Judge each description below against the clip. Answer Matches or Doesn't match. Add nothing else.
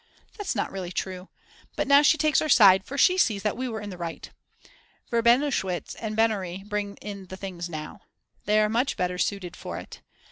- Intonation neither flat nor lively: Matches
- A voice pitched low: Doesn't match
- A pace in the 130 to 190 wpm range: Doesn't match